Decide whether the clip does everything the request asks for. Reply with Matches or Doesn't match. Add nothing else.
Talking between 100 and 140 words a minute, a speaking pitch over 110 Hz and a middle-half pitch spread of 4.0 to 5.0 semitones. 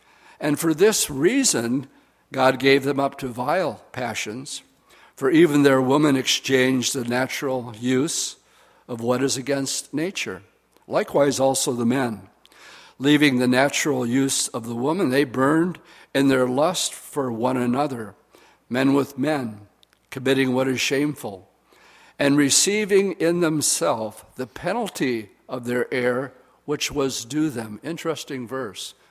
Doesn't match